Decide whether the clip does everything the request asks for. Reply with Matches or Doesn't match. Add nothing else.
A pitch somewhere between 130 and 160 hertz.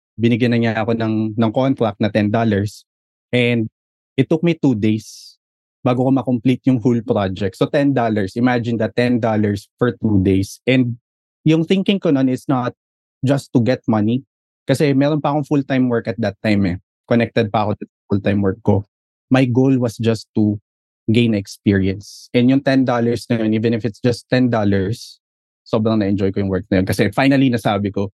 Doesn't match